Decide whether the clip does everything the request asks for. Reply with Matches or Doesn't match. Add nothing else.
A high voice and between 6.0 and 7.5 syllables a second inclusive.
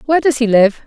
Matches